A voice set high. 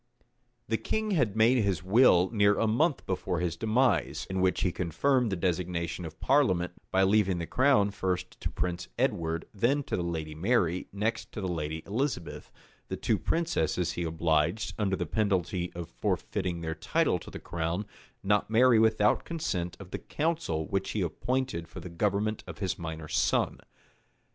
No: very low, 95 Hz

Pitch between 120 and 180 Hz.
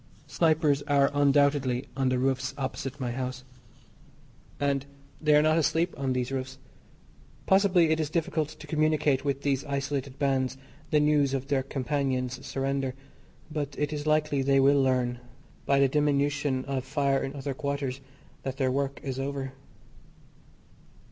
Yes: medium, 140 Hz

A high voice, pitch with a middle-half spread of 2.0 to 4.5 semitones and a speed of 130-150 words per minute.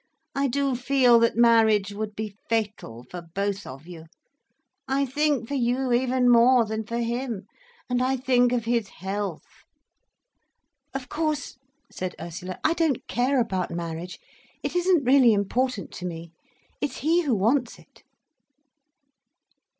No: high, 235 Hz; average, 4.9 semitones; slow, 135 wpm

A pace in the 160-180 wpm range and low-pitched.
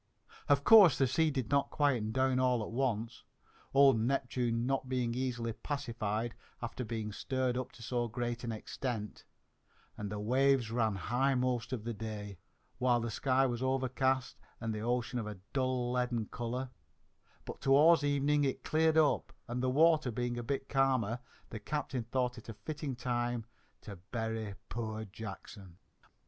Yes: average, 165 wpm; low, 125 Hz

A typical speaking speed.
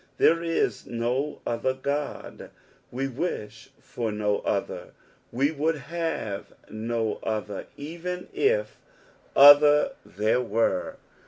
No: slow, 105 wpm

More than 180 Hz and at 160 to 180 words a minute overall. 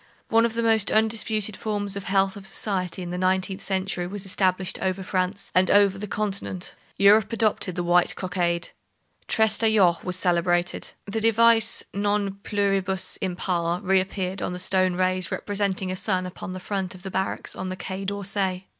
Yes: high, 190 Hz; average, 170 wpm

